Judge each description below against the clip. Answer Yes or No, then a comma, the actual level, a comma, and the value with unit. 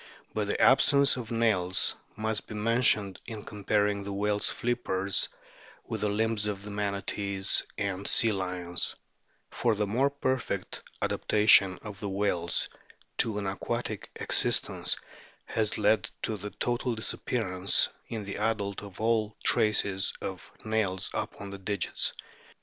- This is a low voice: Yes, low, 105 Hz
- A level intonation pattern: Yes, narrow, 2.0 semitones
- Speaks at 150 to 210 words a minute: No, slow, 135 wpm